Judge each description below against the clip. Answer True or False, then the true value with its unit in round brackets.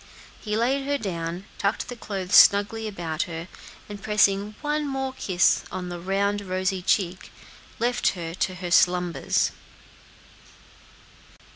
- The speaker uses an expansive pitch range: False (3.6 semitones)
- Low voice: False (195 Hz)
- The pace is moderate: False (130 wpm)